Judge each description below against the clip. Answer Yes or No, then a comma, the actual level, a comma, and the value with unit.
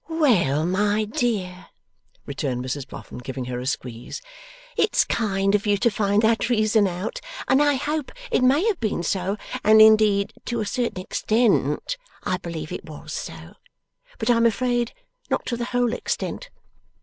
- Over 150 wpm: Yes, average, 165 wpm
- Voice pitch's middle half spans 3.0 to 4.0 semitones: No, average, 5.0 semitones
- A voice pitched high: Yes, high, 210 Hz